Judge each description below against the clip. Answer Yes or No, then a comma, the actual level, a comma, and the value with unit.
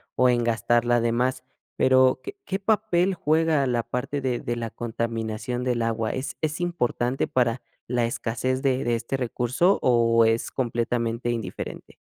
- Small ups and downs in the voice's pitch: Yes, narrow, 2.1 semitones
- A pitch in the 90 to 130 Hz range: Yes, low, 120 Hz